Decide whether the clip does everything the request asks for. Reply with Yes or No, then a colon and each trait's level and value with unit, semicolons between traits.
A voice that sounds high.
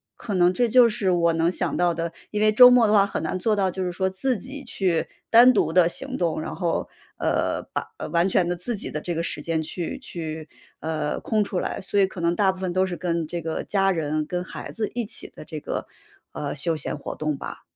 No: medium, 180 Hz